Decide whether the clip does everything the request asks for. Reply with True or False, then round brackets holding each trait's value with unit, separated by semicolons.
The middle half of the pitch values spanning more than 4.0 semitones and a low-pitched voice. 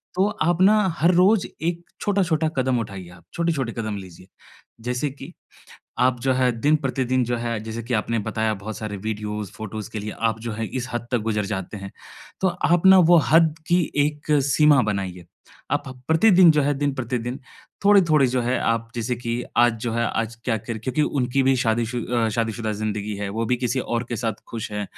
True (5.2 semitones; 120 Hz)